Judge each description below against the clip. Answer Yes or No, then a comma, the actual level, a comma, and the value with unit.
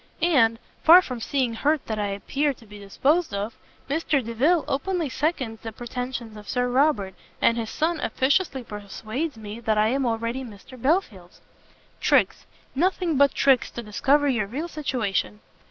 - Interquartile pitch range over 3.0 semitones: Yes, average, 4.8 semitones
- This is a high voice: Yes, very high, 250 Hz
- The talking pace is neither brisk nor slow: Yes, average, 160 wpm